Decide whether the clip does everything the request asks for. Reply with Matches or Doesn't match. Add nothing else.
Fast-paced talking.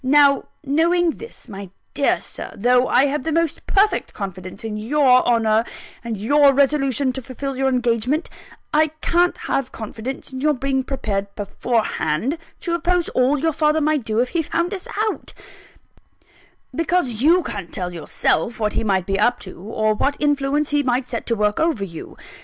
Doesn't match